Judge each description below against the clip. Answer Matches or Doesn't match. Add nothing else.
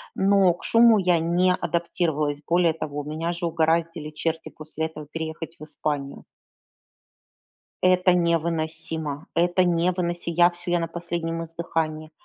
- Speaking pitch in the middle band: Matches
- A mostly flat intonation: Matches